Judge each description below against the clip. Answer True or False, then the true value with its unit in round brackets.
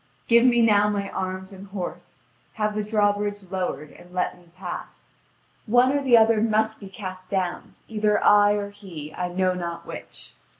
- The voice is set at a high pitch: True (205 Hz)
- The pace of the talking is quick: False (175 wpm)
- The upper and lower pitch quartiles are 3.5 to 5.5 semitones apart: False (2.5 semitones)